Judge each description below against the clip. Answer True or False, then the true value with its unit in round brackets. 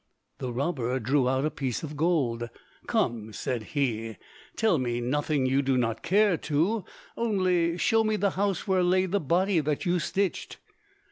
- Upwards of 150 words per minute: True (165 wpm)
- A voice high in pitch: False (150 Hz)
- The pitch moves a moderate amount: False (6.5 semitones)